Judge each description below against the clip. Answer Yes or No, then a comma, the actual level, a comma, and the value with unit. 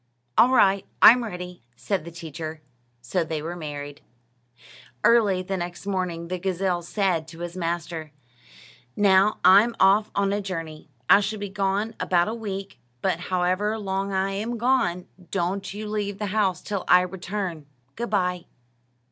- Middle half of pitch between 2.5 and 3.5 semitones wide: Yes, average, 2.8 semitones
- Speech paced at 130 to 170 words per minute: Yes, average, 155 wpm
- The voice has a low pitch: No, high, 190 Hz